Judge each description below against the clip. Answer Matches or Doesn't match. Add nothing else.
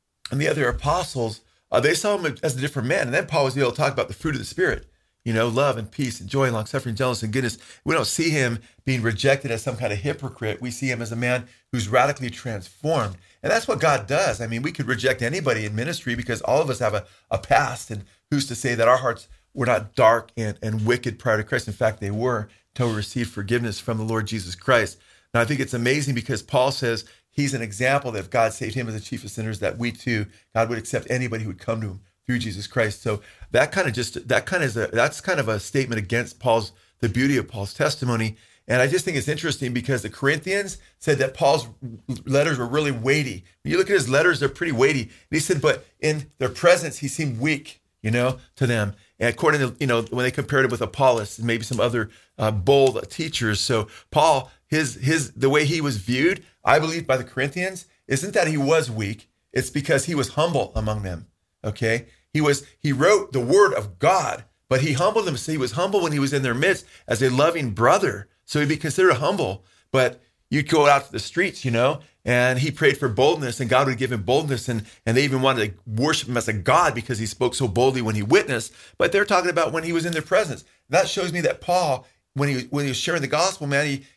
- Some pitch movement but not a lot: Matches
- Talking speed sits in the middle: Doesn't match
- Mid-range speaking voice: Doesn't match